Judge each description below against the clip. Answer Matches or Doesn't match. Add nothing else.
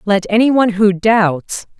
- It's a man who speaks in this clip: Doesn't match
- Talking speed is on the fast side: Doesn't match